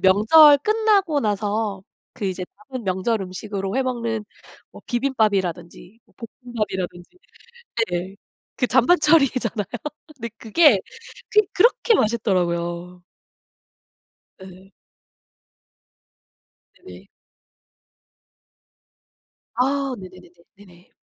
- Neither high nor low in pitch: No, high, 215 Hz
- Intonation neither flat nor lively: No, wide, 5.8 semitones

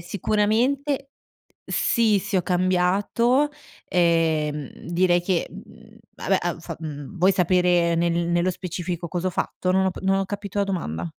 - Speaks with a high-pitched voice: No, medium, 180 Hz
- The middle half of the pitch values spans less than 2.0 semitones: No, average, 2.7 semitones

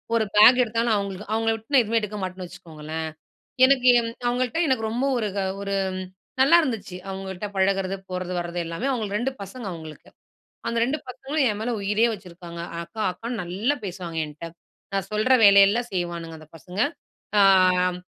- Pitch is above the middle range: Yes, high, 200 Hz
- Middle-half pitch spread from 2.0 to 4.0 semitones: No, average, 4.5 semitones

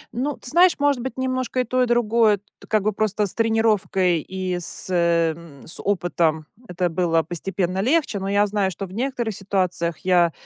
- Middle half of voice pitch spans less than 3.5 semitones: No, average, 4.9 semitones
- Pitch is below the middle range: No, high, 195 Hz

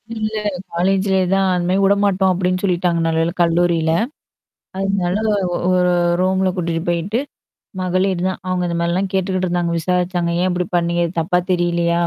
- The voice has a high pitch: No, medium, 180 Hz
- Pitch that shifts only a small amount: Yes, narrow, 1.7 semitones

